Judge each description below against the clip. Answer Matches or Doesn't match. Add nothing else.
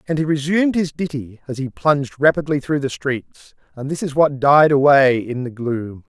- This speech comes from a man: Matches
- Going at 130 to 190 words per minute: Doesn't match